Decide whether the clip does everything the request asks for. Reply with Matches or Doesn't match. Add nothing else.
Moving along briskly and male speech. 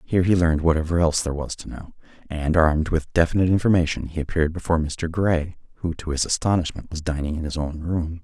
Matches